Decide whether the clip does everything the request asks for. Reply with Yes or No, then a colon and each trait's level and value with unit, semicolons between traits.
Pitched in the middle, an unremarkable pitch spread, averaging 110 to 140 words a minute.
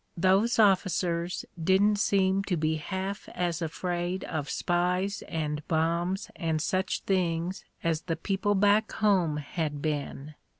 Yes: medium, 180 Hz; average, 3.1 semitones; slow, 135 wpm